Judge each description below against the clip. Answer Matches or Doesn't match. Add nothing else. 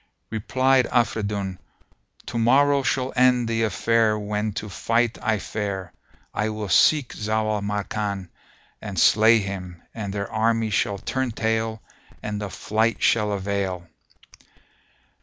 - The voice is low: Matches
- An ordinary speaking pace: Doesn't match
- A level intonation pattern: Matches